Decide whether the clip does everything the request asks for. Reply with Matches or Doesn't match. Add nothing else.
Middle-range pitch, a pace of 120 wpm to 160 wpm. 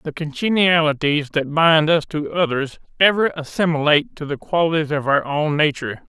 Matches